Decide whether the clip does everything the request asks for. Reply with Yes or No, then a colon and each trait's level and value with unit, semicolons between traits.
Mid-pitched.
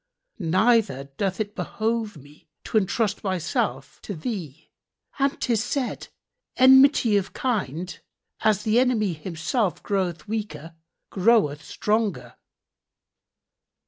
No: high, 205 Hz